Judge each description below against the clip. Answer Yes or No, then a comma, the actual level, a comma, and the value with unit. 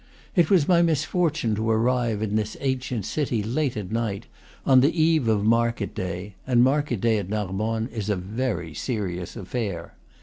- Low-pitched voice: Yes, low, 115 Hz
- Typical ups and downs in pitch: Yes, average, 4.1 semitones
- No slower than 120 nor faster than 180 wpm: Yes, average, 170 wpm